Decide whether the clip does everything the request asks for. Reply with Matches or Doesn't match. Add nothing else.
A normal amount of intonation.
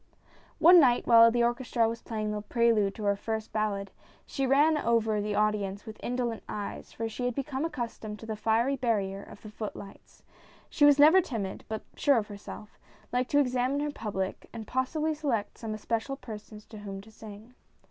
Matches